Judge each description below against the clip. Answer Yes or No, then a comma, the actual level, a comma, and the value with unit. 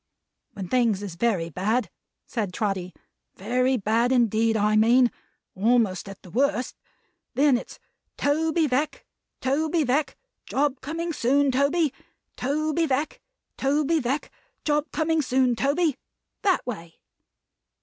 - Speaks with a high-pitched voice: Yes, very high, 255 Hz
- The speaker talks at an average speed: No, slow, 120 wpm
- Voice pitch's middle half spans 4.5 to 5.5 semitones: Yes, average, 5.1 semitones